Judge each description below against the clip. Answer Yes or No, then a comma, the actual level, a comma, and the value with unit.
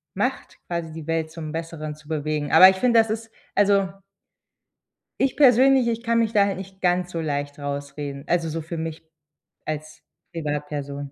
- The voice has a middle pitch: Yes, medium, 165 Hz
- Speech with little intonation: No, average, 4.8 semitones